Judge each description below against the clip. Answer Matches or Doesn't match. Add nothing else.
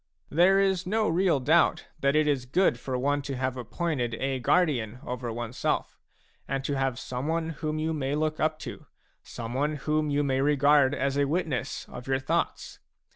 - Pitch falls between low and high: Matches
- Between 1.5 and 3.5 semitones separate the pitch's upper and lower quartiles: Matches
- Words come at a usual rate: Matches